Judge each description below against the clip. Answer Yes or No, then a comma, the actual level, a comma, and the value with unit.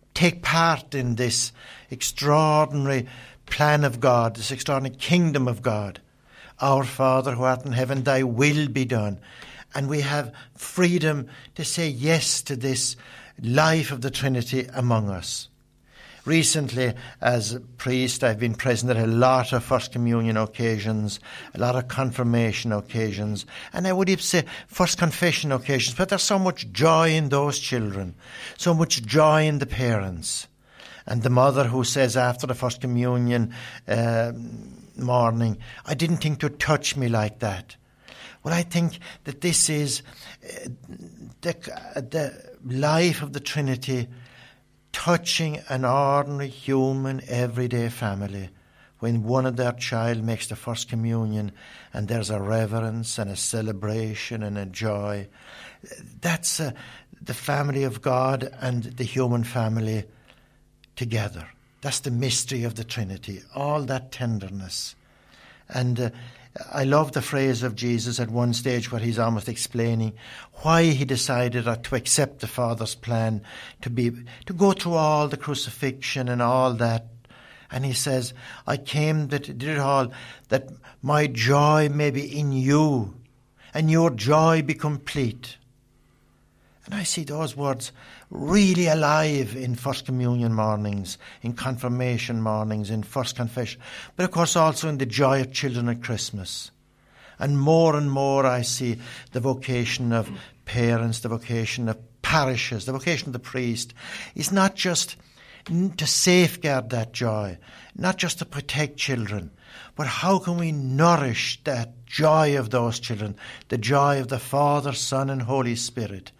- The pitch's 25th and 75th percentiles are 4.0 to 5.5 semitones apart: No, average, 3.6 semitones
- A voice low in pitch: Yes, low, 130 Hz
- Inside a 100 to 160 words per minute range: Yes, average, 150 wpm